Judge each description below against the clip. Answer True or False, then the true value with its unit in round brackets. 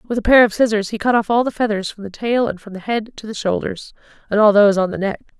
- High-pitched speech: True (210 Hz)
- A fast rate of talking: True (300 wpm)